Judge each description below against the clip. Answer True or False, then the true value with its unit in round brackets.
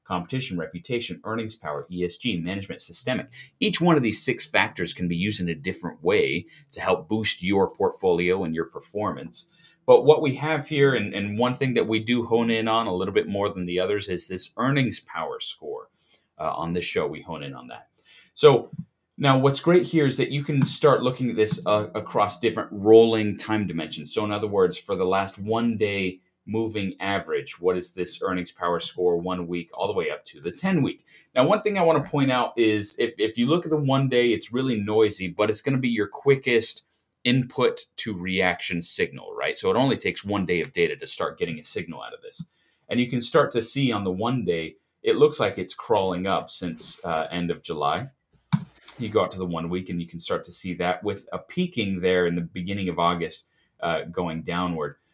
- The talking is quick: True (225 wpm)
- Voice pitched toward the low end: True (110 Hz)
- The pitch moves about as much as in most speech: False (6.9 semitones)